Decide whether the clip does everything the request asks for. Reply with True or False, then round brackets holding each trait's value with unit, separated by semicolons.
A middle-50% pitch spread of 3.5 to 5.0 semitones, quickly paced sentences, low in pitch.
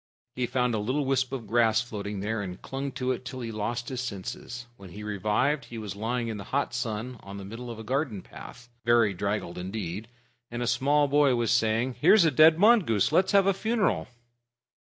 True (4.0 semitones; 210 wpm; 120 Hz)